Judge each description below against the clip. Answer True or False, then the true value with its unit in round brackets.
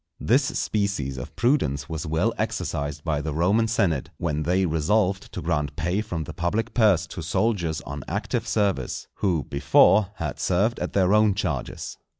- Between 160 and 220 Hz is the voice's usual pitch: False (85 Hz)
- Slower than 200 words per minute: True (165 wpm)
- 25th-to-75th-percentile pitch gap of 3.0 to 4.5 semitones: False (5.1 semitones)